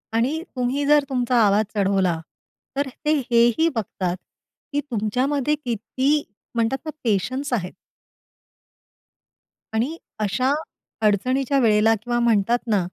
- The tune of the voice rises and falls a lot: No, average, 4.3 semitones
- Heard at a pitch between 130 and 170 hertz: No, high, 240 Hz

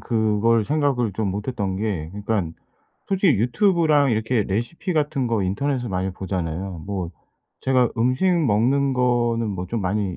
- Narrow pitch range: No, average, 5.2 semitones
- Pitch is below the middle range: Yes, low, 115 Hz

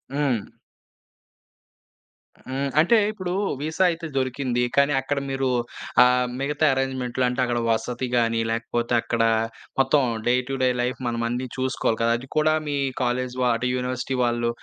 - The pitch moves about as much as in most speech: No, narrow, 2.3 semitones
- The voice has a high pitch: No, low, 130 Hz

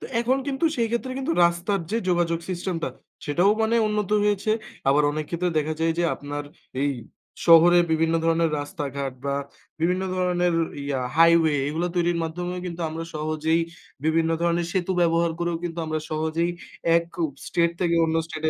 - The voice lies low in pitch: No, medium, 170 Hz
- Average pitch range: No, narrow, 2.0 semitones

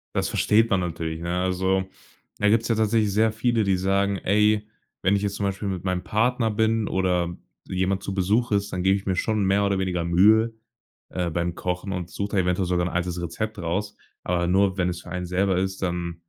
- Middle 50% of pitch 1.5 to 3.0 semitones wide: Yes, narrow, 2.6 semitones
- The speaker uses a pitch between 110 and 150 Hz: No, very low, 95 Hz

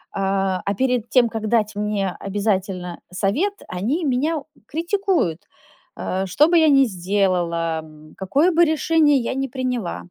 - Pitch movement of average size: No, wide, 7.3 semitones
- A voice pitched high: Yes, high, 215 Hz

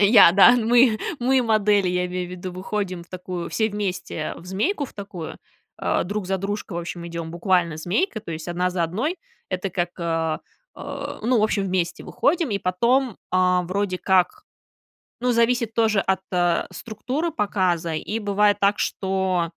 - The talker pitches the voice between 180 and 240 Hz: Yes, high, 190 Hz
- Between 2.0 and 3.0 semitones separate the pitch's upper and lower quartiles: No, average, 3.4 semitones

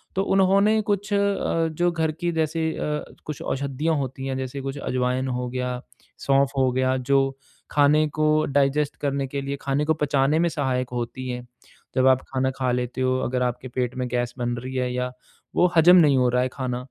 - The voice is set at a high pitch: No, low, 135 Hz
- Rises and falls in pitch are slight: No, average, 3.3 semitones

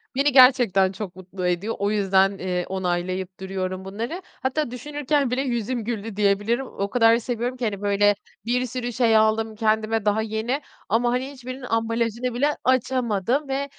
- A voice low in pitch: No, high, 225 Hz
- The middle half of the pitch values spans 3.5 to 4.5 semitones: Yes, average, 4.0 semitones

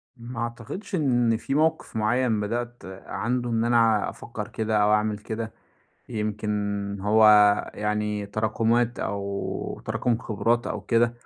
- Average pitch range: No, narrow, 2.1 semitones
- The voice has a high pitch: No, low, 115 Hz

